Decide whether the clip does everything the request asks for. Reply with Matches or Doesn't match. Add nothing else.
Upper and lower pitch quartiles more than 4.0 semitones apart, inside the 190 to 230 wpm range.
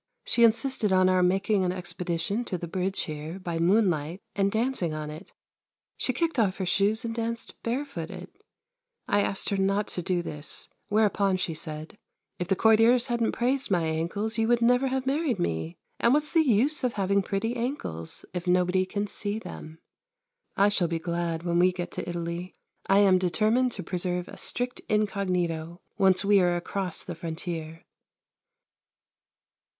Doesn't match